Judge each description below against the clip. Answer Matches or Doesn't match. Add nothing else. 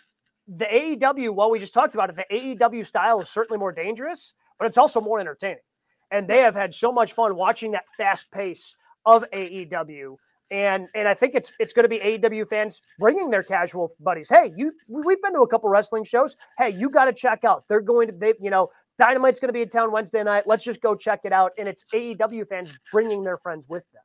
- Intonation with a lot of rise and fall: Doesn't match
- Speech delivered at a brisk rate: Matches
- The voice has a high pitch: Matches